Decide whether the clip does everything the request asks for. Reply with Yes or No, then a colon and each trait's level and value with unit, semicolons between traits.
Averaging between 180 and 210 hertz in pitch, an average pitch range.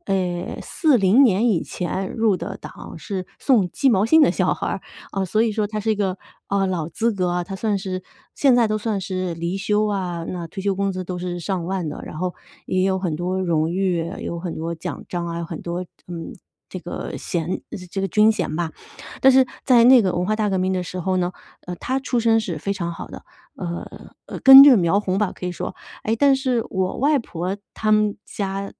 Yes: high, 190 Hz; average, 3.4 semitones